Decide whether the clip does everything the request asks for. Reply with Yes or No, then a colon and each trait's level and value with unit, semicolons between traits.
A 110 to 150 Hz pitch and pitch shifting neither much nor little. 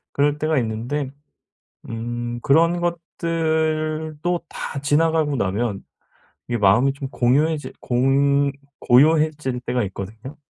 Yes: medium, 140 Hz; average, 4.5 semitones